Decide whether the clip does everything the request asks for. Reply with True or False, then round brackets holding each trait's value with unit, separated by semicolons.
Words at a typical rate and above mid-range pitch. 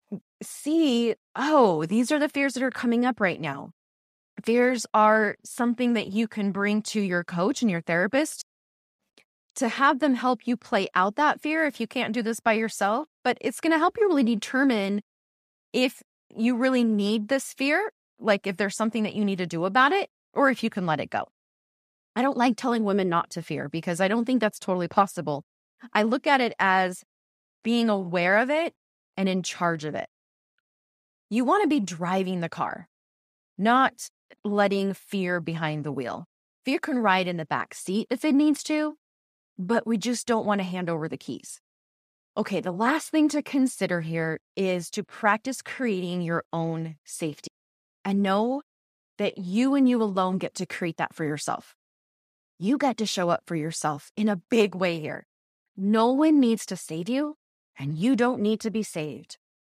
True (190 wpm; 215 Hz)